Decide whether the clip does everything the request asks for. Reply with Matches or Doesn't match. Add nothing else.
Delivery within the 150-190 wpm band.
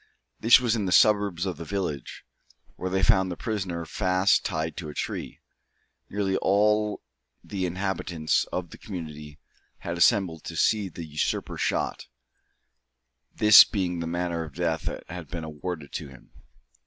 Matches